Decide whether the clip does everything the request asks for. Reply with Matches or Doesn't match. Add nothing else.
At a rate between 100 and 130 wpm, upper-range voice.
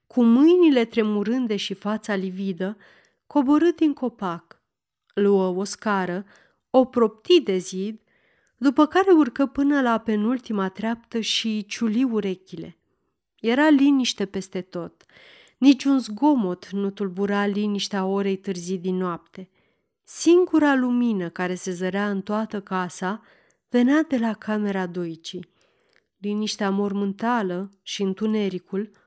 Matches